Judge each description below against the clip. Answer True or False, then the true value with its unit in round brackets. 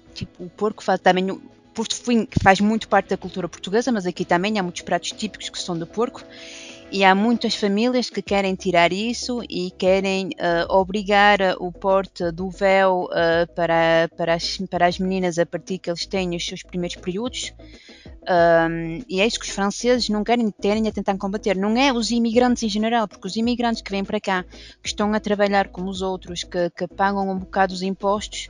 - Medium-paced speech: False (200 wpm)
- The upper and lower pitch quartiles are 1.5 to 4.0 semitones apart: True (2.9 semitones)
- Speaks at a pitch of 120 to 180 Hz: False (195 Hz)